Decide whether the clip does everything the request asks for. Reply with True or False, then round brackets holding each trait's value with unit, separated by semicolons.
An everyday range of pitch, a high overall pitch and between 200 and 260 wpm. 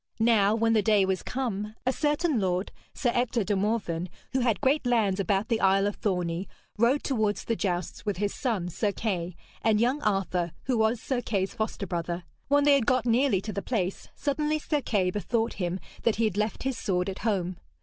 True (4.1 semitones; 215 Hz; 205 wpm)